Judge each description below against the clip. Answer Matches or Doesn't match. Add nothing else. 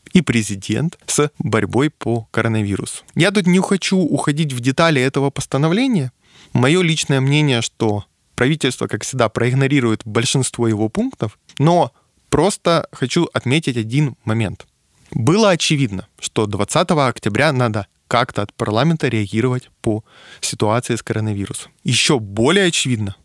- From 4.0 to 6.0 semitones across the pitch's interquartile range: Matches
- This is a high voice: Doesn't match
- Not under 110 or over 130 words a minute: Matches